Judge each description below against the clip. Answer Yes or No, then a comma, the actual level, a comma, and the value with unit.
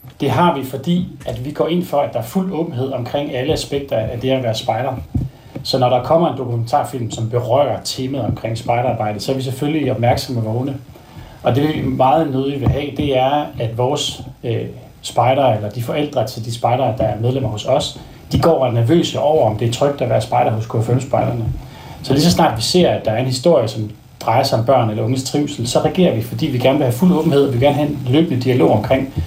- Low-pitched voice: Yes, low, 130 Hz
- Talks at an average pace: No, fast, 240 wpm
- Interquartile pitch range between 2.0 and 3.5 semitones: Yes, average, 3.2 semitones